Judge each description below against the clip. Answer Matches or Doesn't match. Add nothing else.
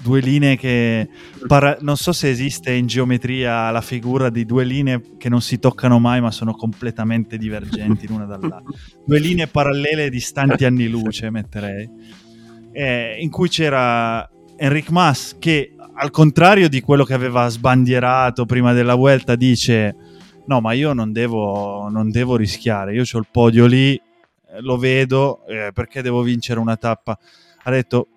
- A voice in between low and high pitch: Doesn't match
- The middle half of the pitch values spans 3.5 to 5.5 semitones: Doesn't match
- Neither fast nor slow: Matches